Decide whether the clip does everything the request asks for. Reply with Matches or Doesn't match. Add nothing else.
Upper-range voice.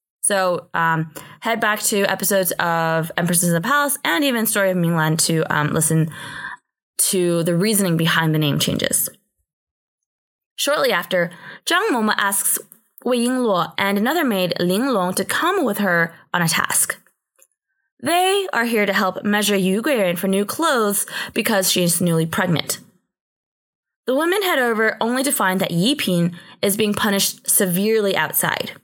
Matches